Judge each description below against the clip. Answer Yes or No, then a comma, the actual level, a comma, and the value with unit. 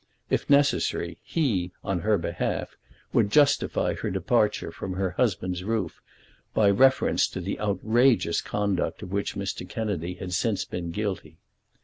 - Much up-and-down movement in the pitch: No, average, 3.7 semitones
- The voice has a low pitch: Yes, low, 100 Hz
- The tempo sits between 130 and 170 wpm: Yes, average, 145 wpm